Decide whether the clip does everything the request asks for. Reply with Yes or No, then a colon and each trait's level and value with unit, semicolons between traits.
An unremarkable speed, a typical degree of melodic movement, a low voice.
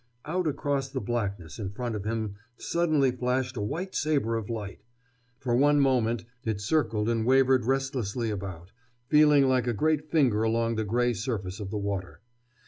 Yes: average, 170 wpm; average, 4.2 semitones; low, 120 Hz